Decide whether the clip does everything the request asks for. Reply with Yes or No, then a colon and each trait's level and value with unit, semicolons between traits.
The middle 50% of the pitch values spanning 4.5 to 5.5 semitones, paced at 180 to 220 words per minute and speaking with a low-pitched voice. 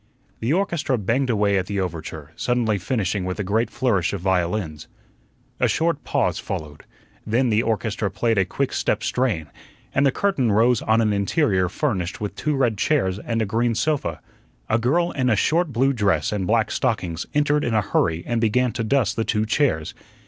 Yes: average, 4.9 semitones; average, 190 wpm; low, 110 Hz